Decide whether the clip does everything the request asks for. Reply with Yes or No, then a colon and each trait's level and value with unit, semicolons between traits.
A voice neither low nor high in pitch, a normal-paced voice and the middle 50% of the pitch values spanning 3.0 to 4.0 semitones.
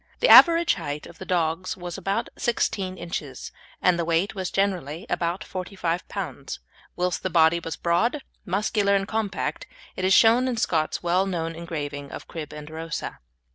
Yes: medium, 180 Hz; average, 170 wpm; average, 3.3 semitones